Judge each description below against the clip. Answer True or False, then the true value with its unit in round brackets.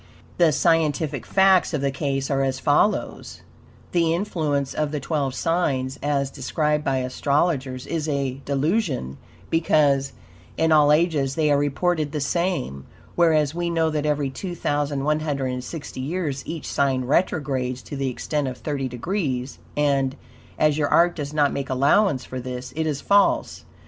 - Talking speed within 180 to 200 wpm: False (150 wpm)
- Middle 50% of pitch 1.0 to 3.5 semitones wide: True (3.0 semitones)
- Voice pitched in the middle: True (145 Hz)